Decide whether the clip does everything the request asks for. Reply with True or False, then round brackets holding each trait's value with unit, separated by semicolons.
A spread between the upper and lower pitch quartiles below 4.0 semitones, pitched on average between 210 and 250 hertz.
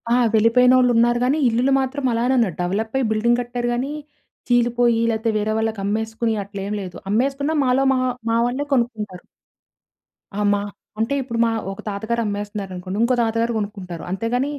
True (2.8 semitones; 230 Hz)